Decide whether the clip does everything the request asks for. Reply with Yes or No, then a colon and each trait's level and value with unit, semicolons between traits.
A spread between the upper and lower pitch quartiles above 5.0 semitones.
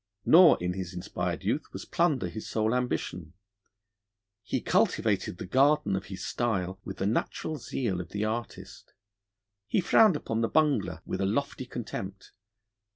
Yes: wide, 5.6 semitones